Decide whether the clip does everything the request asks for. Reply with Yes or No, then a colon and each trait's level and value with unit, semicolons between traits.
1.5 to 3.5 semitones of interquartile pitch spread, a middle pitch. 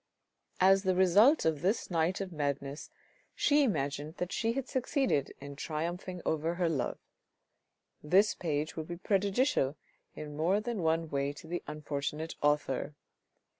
No: average, 4.7 semitones; medium, 165 Hz